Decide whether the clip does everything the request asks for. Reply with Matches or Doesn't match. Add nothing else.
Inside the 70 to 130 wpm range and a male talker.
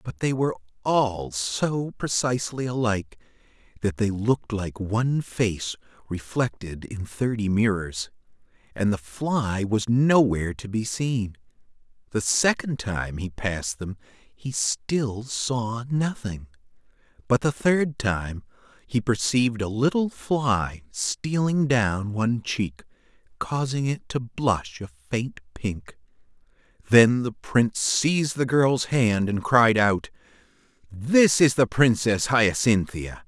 Matches